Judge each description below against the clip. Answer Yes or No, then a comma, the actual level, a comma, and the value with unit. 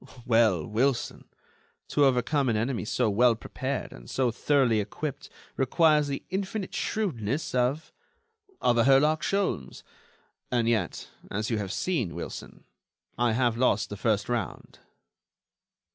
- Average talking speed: No, slow, 130 wpm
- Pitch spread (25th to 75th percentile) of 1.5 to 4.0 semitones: No, average, 4.5 semitones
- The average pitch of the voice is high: No, low, 125 Hz